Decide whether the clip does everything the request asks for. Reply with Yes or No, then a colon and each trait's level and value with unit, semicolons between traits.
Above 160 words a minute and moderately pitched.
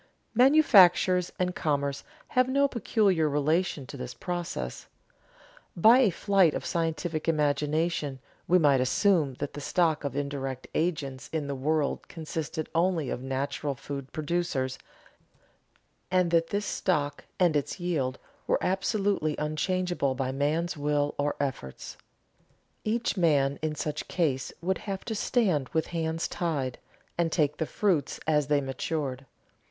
No: slow, 135 wpm; medium, 155 Hz